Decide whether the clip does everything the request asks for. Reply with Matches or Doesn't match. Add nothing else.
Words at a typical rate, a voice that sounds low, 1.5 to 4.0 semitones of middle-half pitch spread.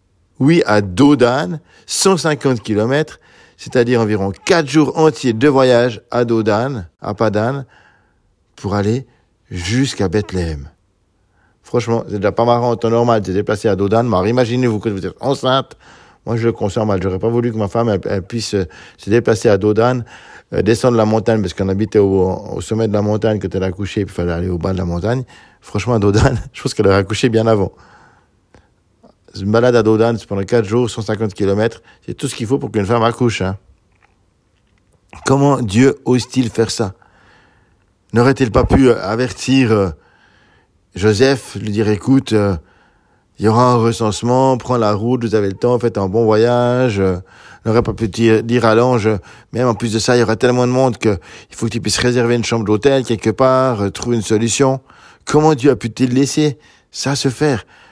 Matches